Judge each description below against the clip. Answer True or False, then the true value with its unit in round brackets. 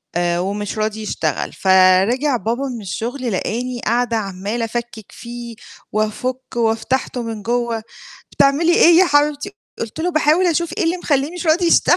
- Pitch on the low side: False (240 Hz)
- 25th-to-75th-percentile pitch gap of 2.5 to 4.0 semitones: False (5.1 semitones)